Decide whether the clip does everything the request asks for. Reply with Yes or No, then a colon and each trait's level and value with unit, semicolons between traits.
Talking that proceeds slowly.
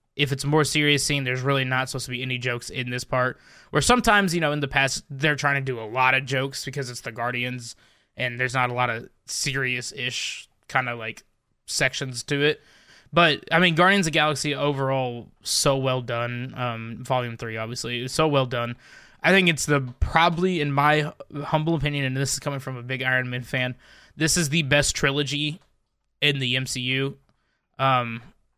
No: average, 200 wpm